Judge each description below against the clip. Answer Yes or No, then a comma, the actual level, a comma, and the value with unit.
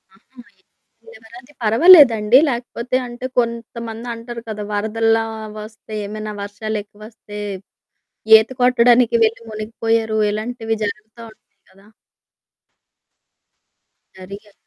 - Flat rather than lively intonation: Yes, narrow, 1.8 semitones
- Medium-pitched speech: No, high, 225 Hz